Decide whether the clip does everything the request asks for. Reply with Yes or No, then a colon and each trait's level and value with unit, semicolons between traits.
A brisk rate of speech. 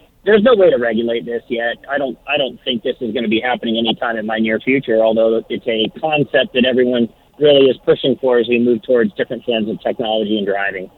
Yes: fast, 235 wpm